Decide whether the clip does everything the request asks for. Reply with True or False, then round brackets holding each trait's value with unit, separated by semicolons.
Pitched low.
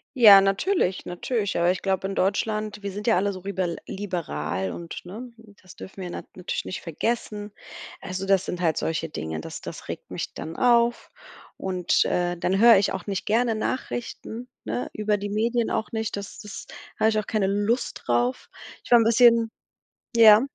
False (200 Hz)